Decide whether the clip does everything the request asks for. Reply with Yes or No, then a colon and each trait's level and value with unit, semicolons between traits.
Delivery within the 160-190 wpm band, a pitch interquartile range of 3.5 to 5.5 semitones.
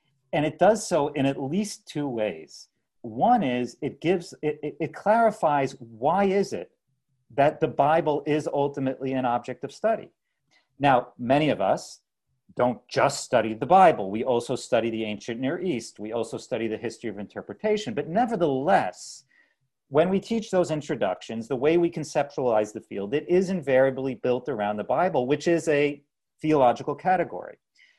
Yes: average, 165 wpm; average, 5.2 semitones